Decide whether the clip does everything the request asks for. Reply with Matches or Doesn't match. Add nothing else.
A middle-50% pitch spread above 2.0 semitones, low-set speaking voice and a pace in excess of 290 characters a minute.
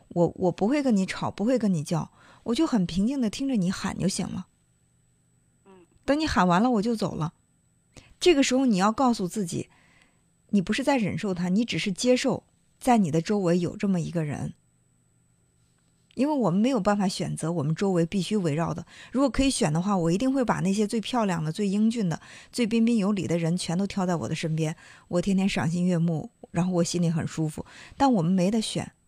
Doesn't match